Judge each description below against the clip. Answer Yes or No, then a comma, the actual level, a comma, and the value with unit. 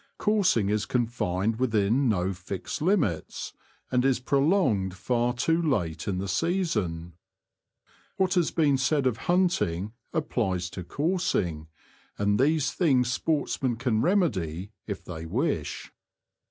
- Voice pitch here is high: No, low, 120 Hz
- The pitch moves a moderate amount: No, wide, 8.5 semitones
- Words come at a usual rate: No, slow, 125 wpm